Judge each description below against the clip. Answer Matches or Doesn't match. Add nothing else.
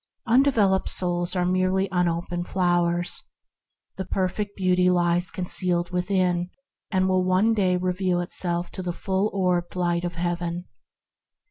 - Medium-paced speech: Doesn't match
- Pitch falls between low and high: Matches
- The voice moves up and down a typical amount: Doesn't match